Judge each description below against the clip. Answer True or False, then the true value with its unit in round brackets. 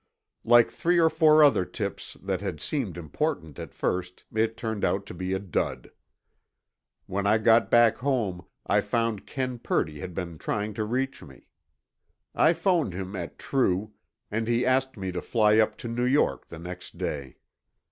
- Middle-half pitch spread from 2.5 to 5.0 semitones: False (5.5 semitones)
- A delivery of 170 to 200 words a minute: True (175 wpm)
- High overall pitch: False (110 Hz)